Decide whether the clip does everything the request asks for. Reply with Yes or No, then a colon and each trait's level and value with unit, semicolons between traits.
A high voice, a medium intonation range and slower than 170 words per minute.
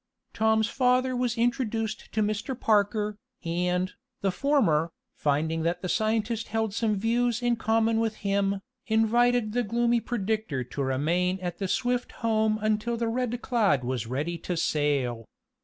Yes: high, 215 Hz; average, 4.7 semitones; average, 150 wpm